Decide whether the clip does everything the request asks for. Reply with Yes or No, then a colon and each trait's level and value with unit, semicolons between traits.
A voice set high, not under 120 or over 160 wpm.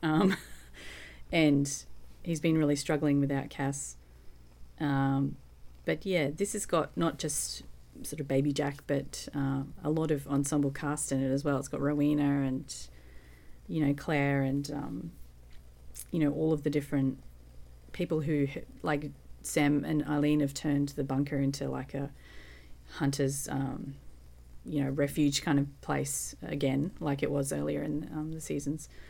No: medium, 140 Hz; average, 155 wpm